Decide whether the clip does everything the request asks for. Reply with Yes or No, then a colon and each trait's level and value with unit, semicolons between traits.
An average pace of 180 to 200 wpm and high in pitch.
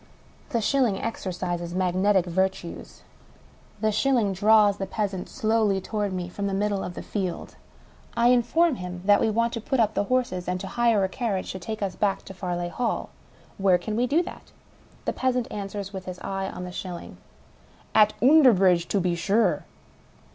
Yes: average, 185 wpm; high, 200 Hz